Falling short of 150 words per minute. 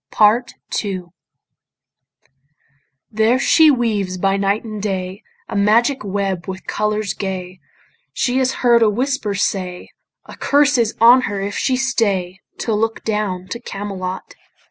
Yes: average, 140 wpm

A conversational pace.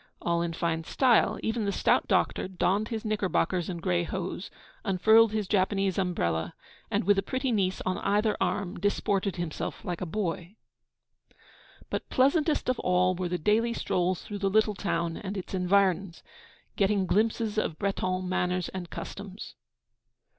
Yes: average, 155 wpm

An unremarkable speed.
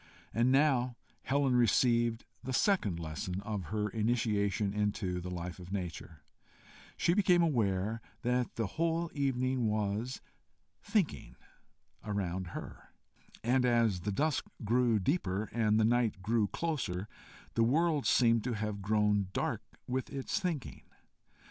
No: slow, 130 wpm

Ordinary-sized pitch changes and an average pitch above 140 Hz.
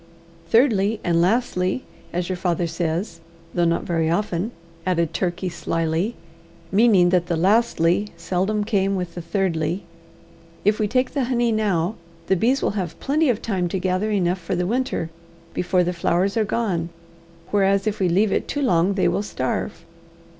Yes: average, 3.7 semitones; medium, 185 Hz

